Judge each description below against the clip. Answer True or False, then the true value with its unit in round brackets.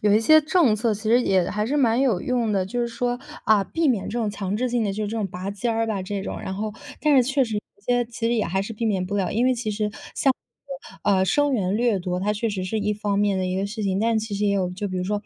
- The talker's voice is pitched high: True (215 Hz)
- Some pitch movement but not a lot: True (3.4 semitones)